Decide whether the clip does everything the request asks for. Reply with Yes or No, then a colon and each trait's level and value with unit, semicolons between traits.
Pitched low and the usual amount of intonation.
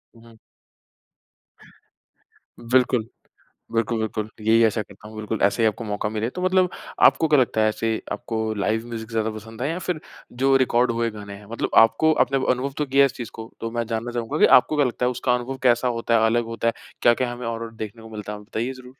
No: low, 115 Hz; narrow, 2.2 semitones